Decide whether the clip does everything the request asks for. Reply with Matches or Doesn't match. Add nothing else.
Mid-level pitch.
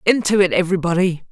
Matches